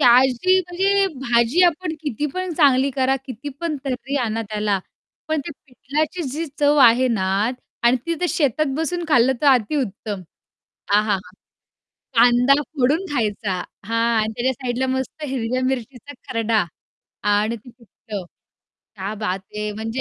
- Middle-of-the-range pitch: No, very high, 255 Hz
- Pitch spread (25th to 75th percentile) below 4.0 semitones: No, average, 4.5 semitones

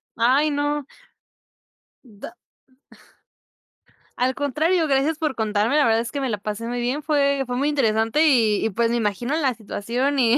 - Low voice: No, very high, 255 Hz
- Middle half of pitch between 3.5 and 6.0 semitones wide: Yes, average, 4.1 semitones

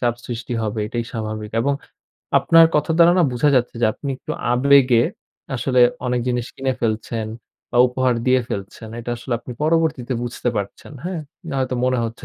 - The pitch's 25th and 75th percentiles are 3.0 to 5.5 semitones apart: No, narrow, 2.4 semitones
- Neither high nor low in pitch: No, low, 125 Hz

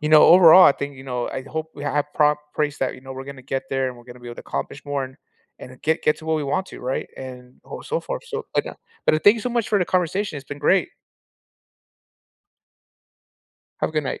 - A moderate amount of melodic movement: Yes, average, 3.7 semitones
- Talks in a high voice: No, medium, 145 Hz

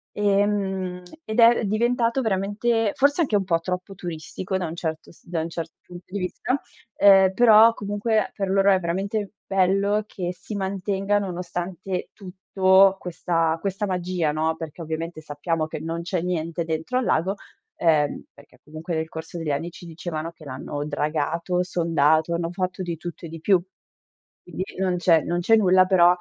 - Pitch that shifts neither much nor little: Yes, average, 3.1 semitones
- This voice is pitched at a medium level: Yes, medium, 180 Hz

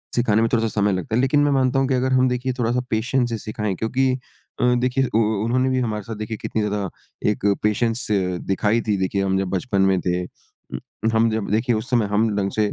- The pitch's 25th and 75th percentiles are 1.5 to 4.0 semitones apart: Yes, average, 3.3 semitones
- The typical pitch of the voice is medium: No, low, 110 Hz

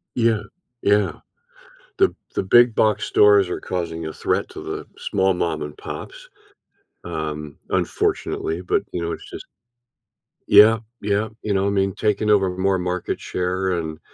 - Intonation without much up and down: No, average, 3.3 semitones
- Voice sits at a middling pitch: No, very low, 95 Hz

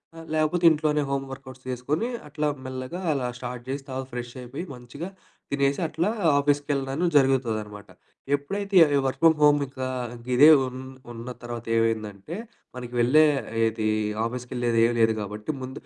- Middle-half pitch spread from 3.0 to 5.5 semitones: Yes, average, 3.5 semitones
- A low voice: Yes, low, 130 Hz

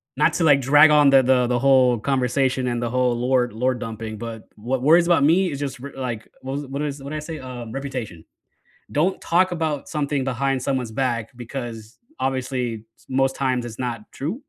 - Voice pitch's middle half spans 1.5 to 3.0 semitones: Yes, average, 2.7 semitones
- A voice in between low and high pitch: No, low, 130 Hz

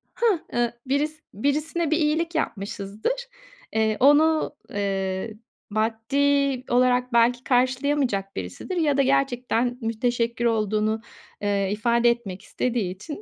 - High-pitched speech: Yes, high, 245 Hz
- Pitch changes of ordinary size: Yes, average, 4.7 semitones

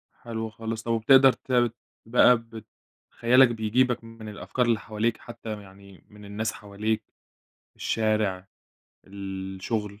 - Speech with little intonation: Yes, narrow, 2.2 semitones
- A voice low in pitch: Yes, low, 110 Hz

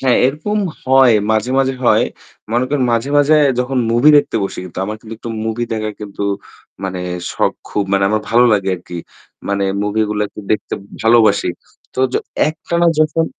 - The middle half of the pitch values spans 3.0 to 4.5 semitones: Yes, average, 4.1 semitones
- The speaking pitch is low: Yes, low, 115 Hz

